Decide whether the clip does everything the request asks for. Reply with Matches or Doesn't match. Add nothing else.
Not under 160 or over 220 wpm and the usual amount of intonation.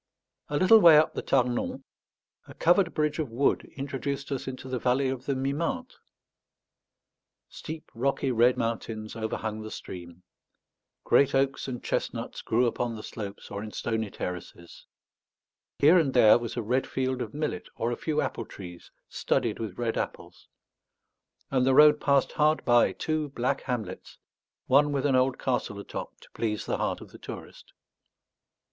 Matches